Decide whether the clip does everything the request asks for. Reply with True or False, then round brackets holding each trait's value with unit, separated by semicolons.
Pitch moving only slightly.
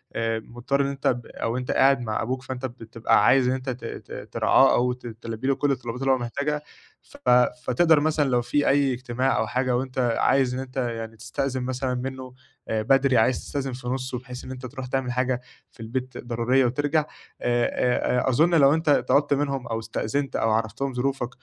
True (2.0 semitones)